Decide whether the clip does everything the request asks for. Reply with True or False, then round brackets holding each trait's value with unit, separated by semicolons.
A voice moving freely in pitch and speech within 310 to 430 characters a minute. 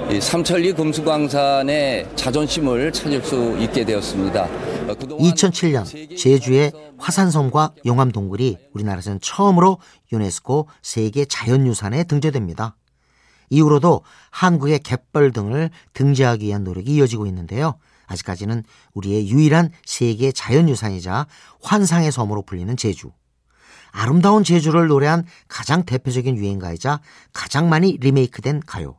True (6.3 semitones; 315 characters per minute)